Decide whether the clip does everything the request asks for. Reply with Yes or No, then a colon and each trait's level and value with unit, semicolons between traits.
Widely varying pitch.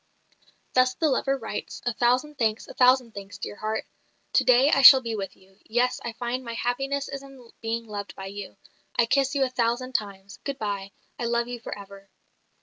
No: average, 3.9 semitones